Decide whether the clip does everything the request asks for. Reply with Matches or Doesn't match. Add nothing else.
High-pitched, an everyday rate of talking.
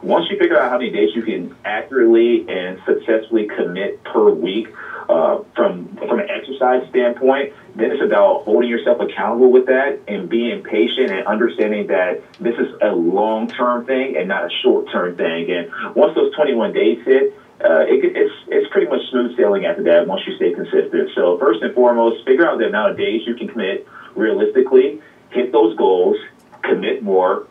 Matches